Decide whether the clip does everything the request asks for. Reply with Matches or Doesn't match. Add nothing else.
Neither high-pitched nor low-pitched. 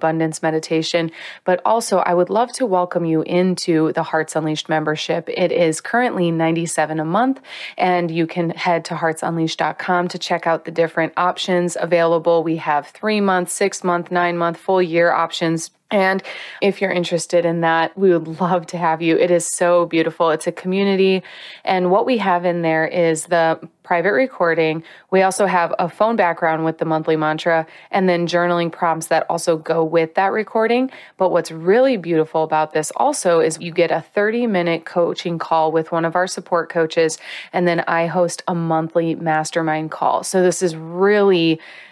Matches